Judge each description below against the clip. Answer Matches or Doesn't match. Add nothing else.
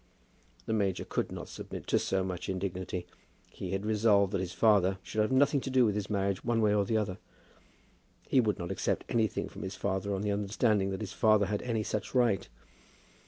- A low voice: Matches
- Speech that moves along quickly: Matches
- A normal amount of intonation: Doesn't match